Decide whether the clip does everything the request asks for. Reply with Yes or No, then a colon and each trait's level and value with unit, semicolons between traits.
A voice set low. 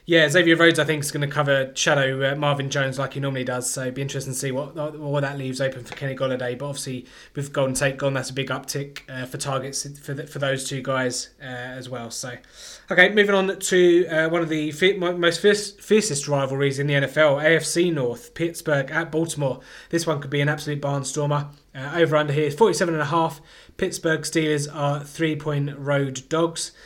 No: medium, 145 Hz